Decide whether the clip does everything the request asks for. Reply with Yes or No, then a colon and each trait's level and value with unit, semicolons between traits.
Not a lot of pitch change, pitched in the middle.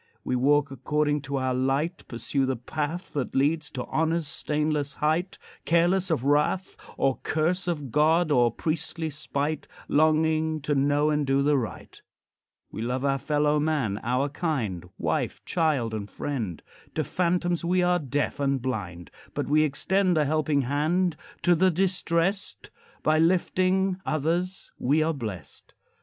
No: average, 3.4 semitones; medium, 150 Hz